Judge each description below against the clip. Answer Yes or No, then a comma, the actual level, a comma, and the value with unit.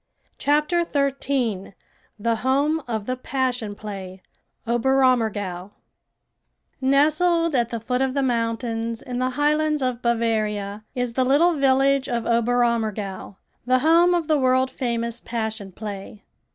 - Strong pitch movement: No, average, 3.6 semitones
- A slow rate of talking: Yes, slow, 125 wpm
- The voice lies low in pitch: No, high, 245 Hz